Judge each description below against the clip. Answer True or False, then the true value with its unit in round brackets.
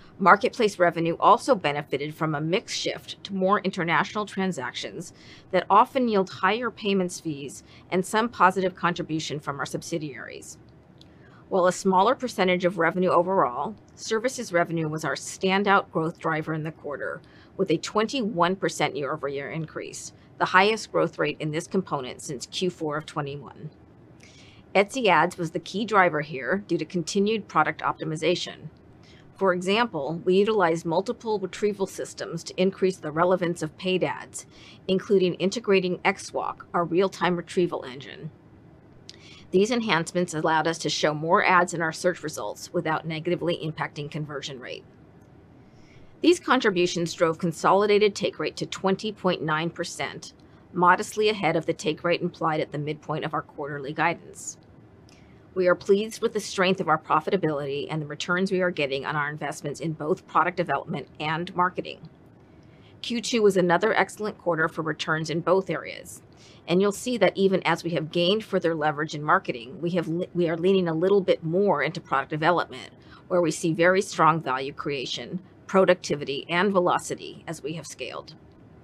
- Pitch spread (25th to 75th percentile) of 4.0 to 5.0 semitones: False (3.3 semitones)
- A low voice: False (175 Hz)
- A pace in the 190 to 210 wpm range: False (155 wpm)